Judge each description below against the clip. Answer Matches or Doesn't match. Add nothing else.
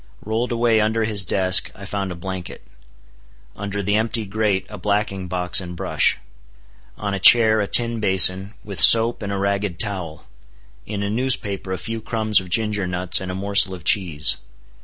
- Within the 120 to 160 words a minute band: Doesn't match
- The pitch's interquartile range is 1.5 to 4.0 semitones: Matches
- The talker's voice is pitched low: Matches